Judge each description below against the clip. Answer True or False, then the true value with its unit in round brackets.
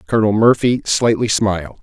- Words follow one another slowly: True (130 wpm)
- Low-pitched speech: True (105 Hz)